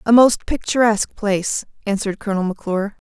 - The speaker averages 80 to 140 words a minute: Yes, slow, 135 wpm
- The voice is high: Yes, high, 210 Hz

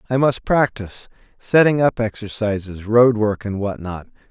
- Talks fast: No, average, 140 wpm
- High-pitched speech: No, low, 110 Hz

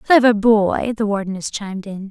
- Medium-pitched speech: No, high, 210 Hz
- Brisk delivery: No, average, 170 wpm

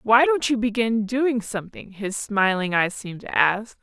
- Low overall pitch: No, high, 220 Hz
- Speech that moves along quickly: No, average, 190 wpm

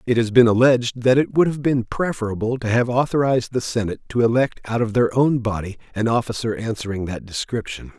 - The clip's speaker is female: No, male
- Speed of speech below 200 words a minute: No, fast, 205 wpm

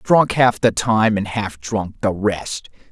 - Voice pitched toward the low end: Yes, low, 105 Hz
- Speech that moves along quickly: No, average, 185 wpm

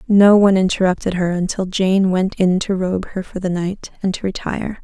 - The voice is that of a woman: Yes, female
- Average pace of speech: No, fast, 210 wpm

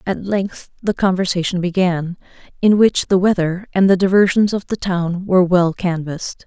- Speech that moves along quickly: No, average, 165 wpm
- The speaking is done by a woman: Yes, female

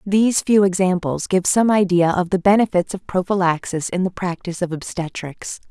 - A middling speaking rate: Yes, average, 170 wpm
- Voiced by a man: No, female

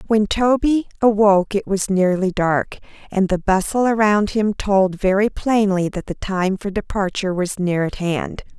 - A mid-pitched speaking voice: No, high, 200 Hz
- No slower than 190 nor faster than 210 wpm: No, average, 170 wpm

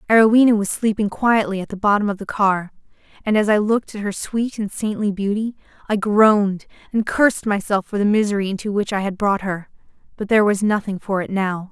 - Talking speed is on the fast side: Yes, fast, 210 wpm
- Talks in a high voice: Yes, high, 205 Hz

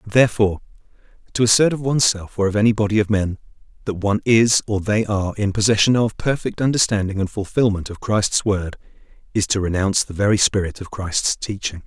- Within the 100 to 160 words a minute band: No, average, 190 wpm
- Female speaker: No, male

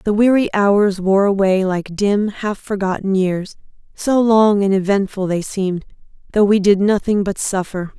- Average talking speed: Yes, average, 165 wpm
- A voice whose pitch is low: No, high, 200 Hz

